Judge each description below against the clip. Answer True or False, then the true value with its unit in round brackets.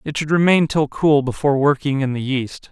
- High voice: False (145 Hz)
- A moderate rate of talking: False (220 wpm)